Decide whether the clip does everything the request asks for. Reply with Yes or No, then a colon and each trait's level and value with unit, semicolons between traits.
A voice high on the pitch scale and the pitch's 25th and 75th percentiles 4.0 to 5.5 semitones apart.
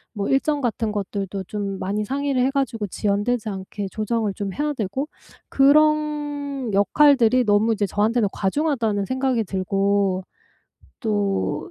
Yes: high, 220 Hz; average, 5.2 semitones